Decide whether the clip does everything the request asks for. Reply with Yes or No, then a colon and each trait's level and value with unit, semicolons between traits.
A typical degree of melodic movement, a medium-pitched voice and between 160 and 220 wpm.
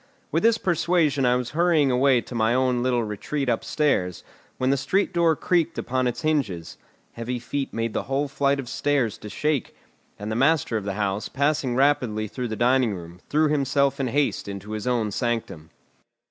No: average, 4.3 semitones; low, 130 Hz; average, 190 wpm